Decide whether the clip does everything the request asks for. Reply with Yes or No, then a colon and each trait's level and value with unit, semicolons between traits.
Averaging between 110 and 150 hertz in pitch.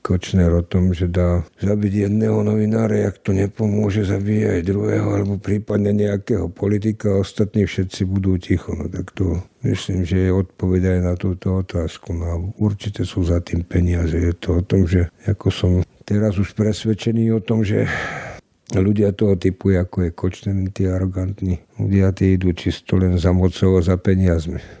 No: very low, 95 Hz